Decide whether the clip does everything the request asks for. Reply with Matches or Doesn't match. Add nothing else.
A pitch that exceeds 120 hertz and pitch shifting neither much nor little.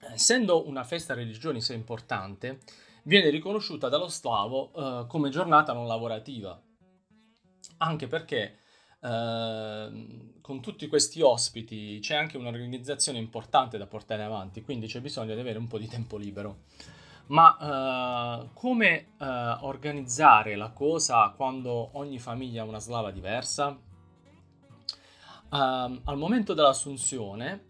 Matches